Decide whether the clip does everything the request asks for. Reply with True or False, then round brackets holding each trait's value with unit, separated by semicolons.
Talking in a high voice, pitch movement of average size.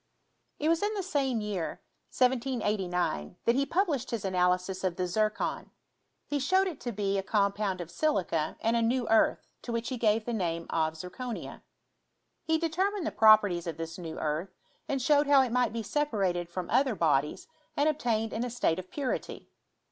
False (220 Hz; 6.7 semitones)